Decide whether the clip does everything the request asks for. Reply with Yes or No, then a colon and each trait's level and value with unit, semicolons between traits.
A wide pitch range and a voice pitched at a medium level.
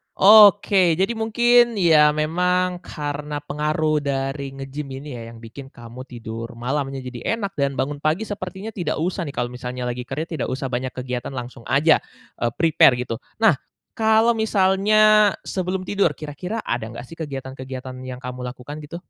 Yes: wide, 6.5 semitones; medium, 150 Hz